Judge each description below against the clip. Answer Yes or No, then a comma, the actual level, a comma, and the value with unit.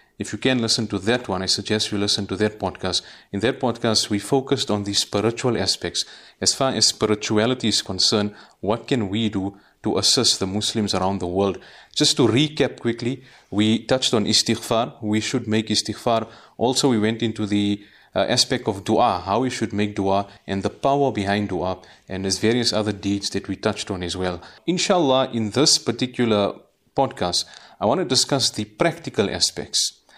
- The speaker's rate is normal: Yes, average, 185 wpm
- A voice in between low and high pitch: No, low, 110 Hz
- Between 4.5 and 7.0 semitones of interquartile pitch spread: No, average, 3.2 semitones